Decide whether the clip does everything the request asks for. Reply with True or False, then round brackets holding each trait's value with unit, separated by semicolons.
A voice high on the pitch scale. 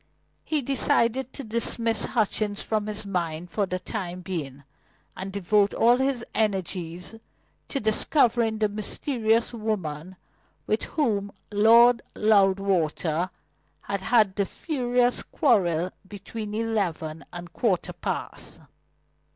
True (210 Hz)